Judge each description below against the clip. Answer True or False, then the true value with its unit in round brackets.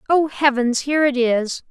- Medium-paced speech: True (175 wpm)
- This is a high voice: True (265 Hz)